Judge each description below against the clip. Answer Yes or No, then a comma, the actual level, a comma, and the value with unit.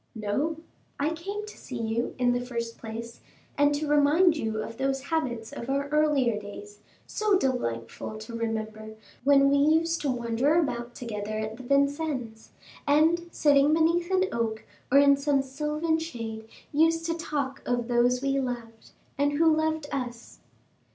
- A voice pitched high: Yes, very high, 275 Hz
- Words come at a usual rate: Yes, average, 160 wpm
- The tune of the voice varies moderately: Yes, average, 4.9 semitones